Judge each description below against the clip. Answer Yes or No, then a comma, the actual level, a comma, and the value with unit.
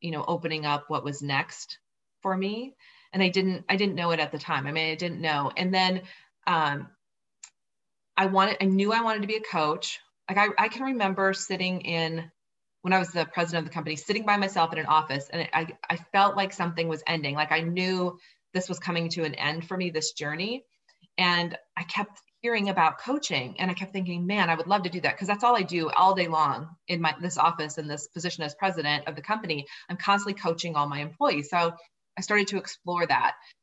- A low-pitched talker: No, medium, 175 Hz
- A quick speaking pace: Yes, fast, 230 wpm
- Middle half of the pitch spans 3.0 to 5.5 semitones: Yes, average, 3.3 semitones